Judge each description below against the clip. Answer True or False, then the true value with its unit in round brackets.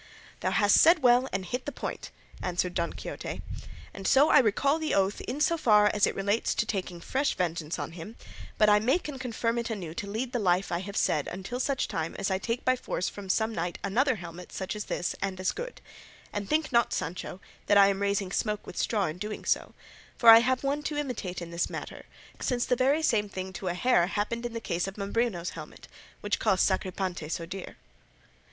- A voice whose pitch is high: True (205 Hz)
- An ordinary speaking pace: False (220 wpm)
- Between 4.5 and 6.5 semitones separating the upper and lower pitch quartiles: True (4.9 semitones)